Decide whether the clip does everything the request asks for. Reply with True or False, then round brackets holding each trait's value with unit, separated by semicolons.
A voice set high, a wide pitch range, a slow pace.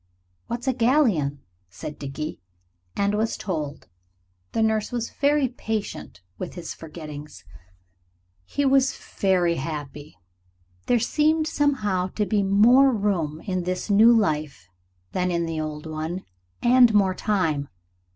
True (195 Hz; 7.0 semitones; 130 wpm)